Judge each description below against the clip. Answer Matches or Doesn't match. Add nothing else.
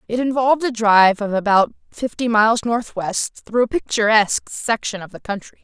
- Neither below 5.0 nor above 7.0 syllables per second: Matches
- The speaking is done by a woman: Matches